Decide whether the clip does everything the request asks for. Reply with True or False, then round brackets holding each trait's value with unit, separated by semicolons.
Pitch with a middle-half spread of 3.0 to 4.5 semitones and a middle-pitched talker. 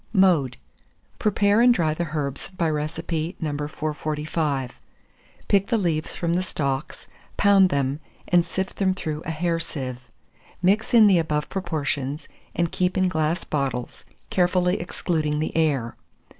True (3.4 semitones; 160 Hz)